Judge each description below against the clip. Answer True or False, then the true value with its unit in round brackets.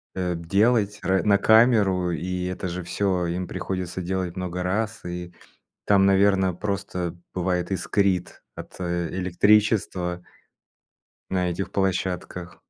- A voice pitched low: True (90 Hz)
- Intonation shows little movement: True (1.9 semitones)